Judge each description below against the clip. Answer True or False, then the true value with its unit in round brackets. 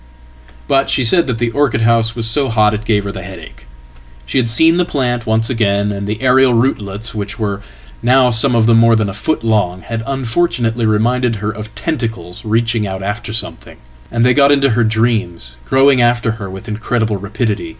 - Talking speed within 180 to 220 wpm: True (185 wpm)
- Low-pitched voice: True (115 Hz)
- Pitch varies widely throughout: False (3.0 semitones)